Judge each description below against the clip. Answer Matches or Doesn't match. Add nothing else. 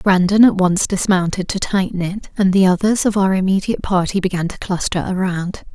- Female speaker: Matches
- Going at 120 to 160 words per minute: Doesn't match